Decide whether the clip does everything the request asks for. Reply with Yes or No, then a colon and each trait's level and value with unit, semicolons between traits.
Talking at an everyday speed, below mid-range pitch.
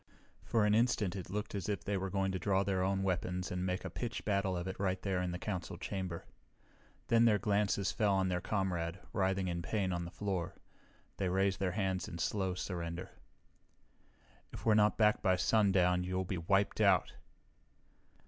Yes: average, 190 wpm; very low, 95 Hz